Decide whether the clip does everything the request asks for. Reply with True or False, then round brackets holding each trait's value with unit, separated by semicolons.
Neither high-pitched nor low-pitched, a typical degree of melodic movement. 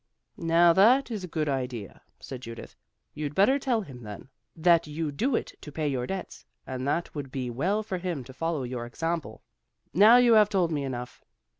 False (155 Hz; 6.6 semitones)